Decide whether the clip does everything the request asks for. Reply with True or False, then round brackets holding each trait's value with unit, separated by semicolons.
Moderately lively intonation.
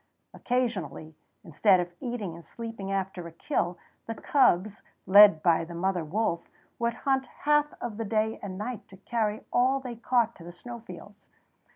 True (5.0 semitones)